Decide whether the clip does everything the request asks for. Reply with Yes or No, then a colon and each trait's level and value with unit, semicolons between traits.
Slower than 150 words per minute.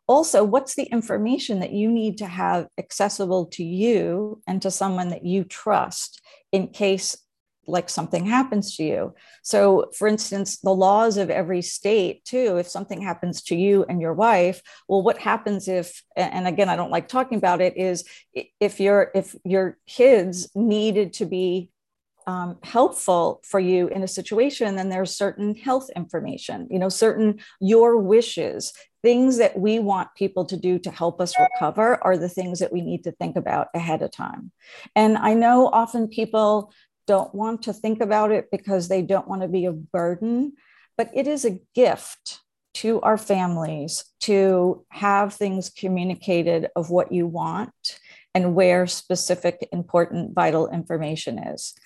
No: average, 165 wpm